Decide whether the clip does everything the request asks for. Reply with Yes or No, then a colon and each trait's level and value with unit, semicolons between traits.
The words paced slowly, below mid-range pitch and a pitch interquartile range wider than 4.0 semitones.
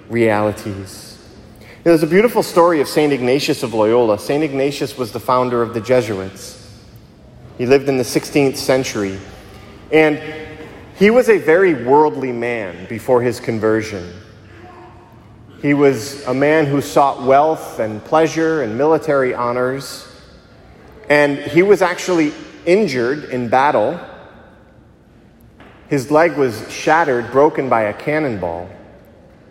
Yes: slow, 125 wpm; low, 130 Hz; wide, 5.4 semitones